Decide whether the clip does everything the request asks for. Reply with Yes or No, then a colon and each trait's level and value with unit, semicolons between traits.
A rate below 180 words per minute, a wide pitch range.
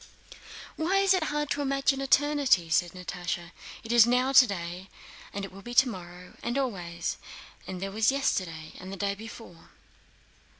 Yes: average, 160 wpm; wide, 7.2 semitones